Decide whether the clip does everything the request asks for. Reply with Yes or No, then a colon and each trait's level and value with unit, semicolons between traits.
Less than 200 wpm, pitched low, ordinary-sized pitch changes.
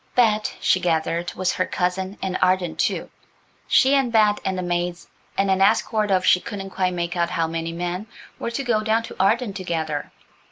No: average, 190 wpm; medium, 185 Hz; average, 3.4 semitones